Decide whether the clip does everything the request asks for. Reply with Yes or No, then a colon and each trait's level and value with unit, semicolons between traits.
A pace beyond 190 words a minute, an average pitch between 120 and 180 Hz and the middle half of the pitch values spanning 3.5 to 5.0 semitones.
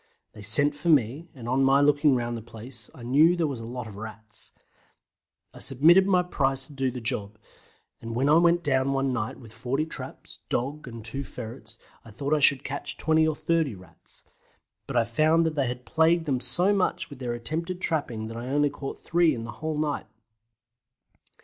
Yes: fast, 205 wpm; low, 135 Hz; average, 4.7 semitones